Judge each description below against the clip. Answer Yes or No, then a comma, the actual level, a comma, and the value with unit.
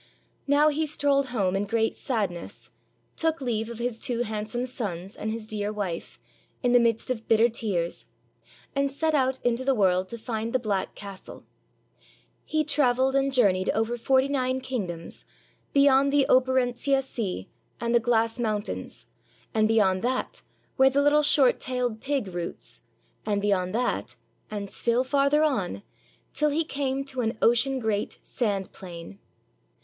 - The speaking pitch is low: No, high, 235 Hz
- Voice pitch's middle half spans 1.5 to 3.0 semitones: No, average, 4.4 semitones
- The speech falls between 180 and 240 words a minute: No, average, 160 wpm